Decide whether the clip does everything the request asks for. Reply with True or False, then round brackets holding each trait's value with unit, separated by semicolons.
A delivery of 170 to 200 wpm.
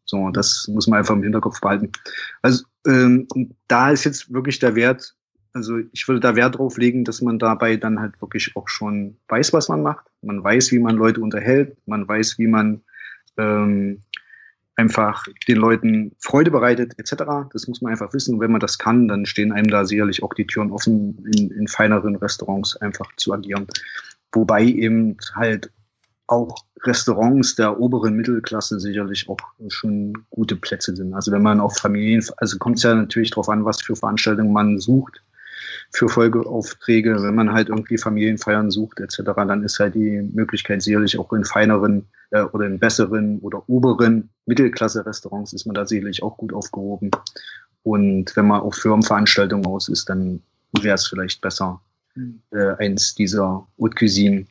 True (175 wpm)